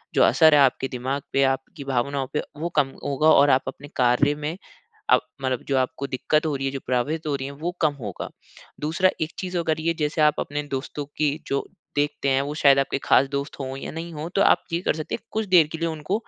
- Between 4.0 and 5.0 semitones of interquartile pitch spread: No, average, 2.7 semitones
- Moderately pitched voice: Yes, medium, 145 Hz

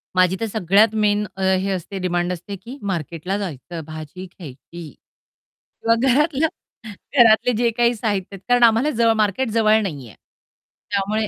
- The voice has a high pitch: Yes, high, 200 Hz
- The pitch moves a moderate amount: Yes, average, 4.2 semitones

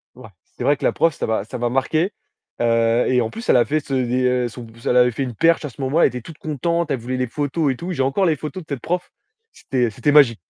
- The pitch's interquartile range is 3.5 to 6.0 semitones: Yes, average, 4.2 semitones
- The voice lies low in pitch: Yes, low, 130 Hz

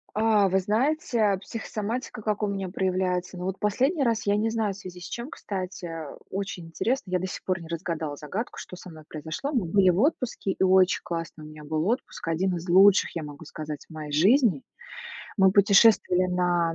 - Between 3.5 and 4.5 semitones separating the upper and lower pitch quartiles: Yes, average, 3.8 semitones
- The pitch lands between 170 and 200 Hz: Yes, high, 190 Hz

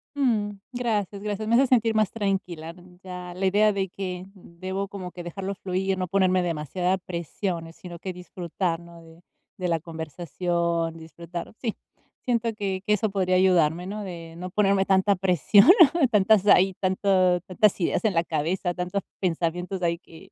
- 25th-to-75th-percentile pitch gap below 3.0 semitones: Yes, narrow, 2.5 semitones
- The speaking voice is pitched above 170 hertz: Yes, medium, 185 Hz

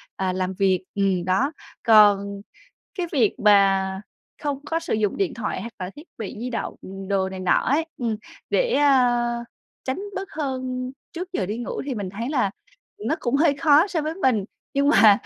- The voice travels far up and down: Yes, wide, 6.5 semitones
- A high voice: Yes, high, 240 Hz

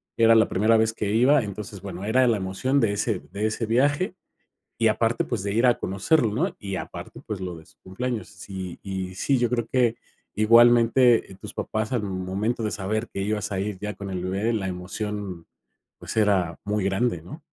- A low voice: Yes, low, 105 Hz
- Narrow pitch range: No, average, 3.5 semitones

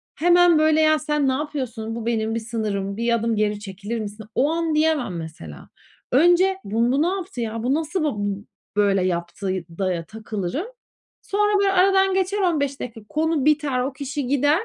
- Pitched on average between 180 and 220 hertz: No, very high, 260 Hz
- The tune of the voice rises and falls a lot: Yes, wide, 6.6 semitones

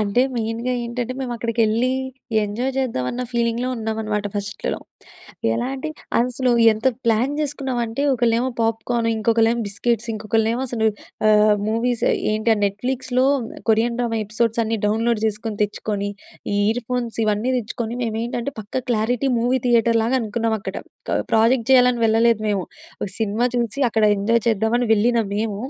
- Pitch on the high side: Yes, high, 230 Hz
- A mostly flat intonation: Yes, narrow, 1.9 semitones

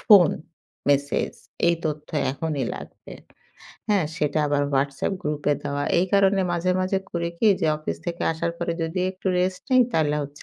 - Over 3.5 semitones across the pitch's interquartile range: Yes, average, 4.0 semitones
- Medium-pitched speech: Yes, medium, 160 Hz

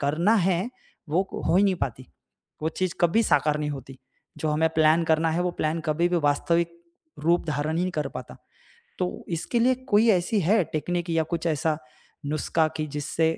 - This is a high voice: No, medium, 165 Hz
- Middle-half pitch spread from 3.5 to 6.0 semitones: No, narrow, 2.6 semitones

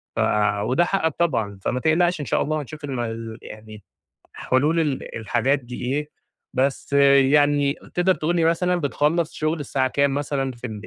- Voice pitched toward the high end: No, medium, 140 Hz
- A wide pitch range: No, average, 4.0 semitones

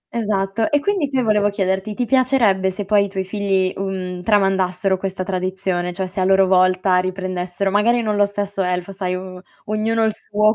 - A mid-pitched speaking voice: No, high, 195 Hz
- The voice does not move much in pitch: Yes, narrow, 2.3 semitones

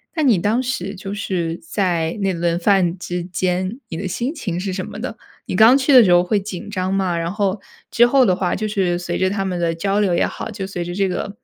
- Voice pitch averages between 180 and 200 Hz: Yes, high, 190 Hz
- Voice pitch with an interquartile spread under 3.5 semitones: Yes, average, 3.0 semitones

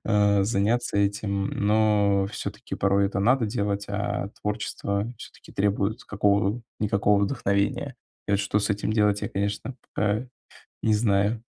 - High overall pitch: No, low, 100 Hz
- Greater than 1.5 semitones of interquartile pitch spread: No, narrow, 1.2 semitones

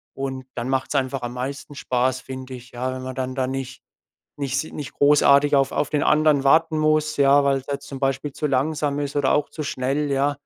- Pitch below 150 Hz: Yes, medium, 140 Hz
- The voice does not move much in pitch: Yes, narrow, 1.8 semitones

